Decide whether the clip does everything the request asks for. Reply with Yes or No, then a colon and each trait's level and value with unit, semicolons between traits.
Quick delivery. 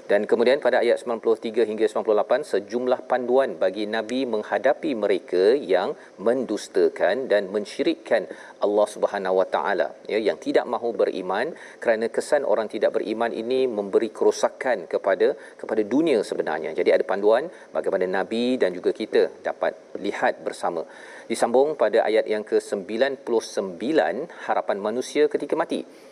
Yes: fast, 130 wpm